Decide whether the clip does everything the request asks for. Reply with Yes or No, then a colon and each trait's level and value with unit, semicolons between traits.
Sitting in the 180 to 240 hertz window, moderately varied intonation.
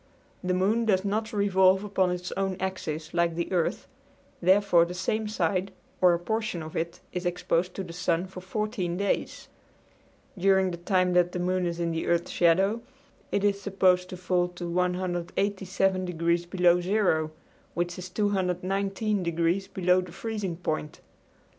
No: medium, 185 Hz; narrow, 2.0 semitones